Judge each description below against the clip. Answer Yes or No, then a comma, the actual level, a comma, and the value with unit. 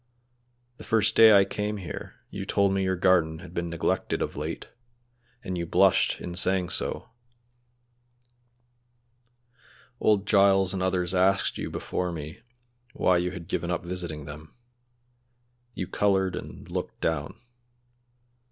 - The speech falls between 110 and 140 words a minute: Yes, slow, 135 wpm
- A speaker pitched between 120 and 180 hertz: No, very low, 90 Hz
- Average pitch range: No, narrow, 2.3 semitones